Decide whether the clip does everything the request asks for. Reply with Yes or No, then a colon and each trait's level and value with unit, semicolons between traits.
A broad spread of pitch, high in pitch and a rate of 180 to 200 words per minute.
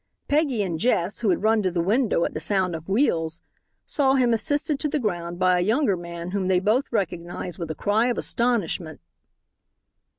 Yes: wide, 5.7 semitones; high, 195 Hz; average, 195 wpm